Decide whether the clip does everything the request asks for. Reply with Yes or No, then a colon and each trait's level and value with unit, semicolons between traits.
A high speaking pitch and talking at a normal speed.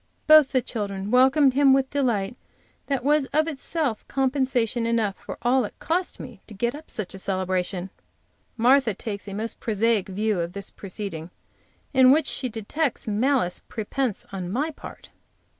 Yes: high, 235 Hz; average, 160 wpm